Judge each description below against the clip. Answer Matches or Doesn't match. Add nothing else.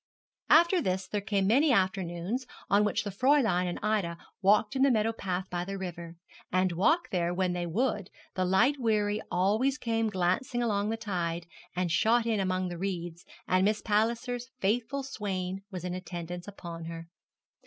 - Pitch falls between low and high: Doesn't match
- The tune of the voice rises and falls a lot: Doesn't match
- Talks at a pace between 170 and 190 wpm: Matches